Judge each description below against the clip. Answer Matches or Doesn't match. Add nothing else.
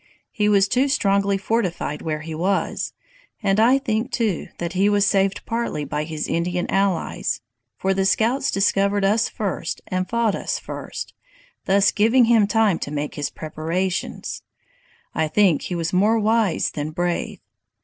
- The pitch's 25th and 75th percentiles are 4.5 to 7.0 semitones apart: Doesn't match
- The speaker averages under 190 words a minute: Matches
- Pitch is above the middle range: Matches